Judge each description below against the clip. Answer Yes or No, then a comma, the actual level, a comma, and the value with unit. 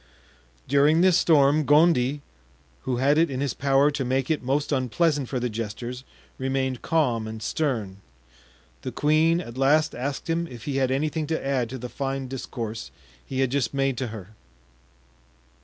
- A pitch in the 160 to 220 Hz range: No, low, 135 Hz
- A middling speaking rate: Yes, average, 170 wpm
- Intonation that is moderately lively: Yes, average, 3.0 semitones